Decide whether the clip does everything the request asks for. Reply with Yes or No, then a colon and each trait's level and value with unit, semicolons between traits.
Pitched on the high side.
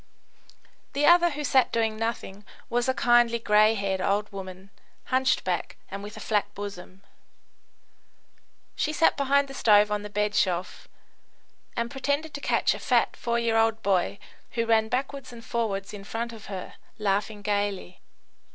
Yes: high, 220 Hz